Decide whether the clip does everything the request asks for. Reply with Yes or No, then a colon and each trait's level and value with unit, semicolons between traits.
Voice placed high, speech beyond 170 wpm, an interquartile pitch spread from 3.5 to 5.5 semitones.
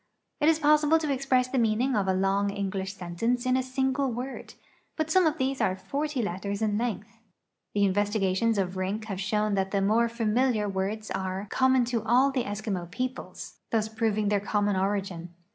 Yes: high, 215 Hz; average, 190 wpm; average, 4.6 semitones